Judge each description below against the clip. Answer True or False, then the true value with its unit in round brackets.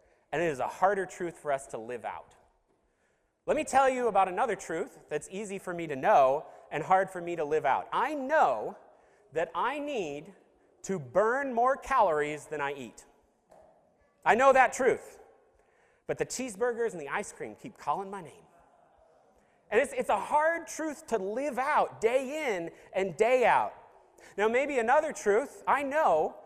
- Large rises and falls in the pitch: True (7.8 semitones)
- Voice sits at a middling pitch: False (235 Hz)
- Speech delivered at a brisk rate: False (175 wpm)